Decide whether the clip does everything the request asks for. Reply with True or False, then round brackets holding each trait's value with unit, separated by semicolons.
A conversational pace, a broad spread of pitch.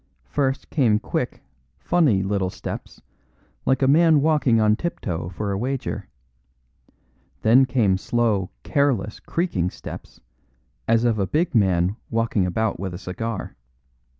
False (130 wpm; 5.7 semitones)